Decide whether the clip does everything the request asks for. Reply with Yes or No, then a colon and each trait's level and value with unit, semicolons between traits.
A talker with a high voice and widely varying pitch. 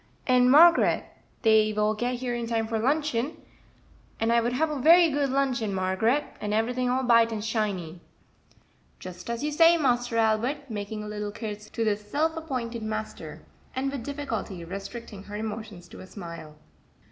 No: high, 230 Hz; average, 3.7 semitones